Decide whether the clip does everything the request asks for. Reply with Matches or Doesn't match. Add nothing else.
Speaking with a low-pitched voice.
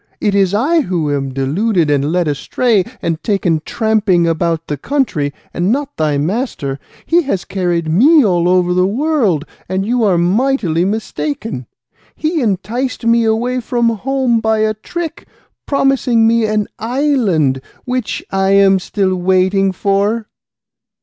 Doesn't match